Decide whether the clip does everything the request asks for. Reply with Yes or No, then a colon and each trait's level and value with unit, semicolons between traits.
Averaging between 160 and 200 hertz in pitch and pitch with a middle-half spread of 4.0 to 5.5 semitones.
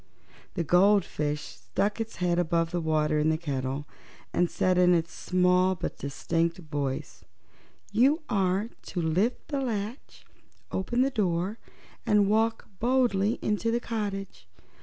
Yes: medium, 185 Hz; average, 4.7 semitones